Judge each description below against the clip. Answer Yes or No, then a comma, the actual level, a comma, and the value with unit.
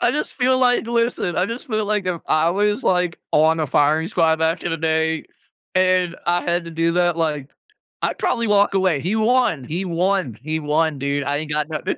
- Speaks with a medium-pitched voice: Yes, medium, 170 Hz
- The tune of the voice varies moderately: Yes, average, 4.0 semitones